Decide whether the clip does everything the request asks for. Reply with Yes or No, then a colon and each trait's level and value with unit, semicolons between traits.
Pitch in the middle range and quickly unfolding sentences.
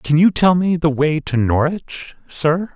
No: medium, 160 Hz; average, 195 wpm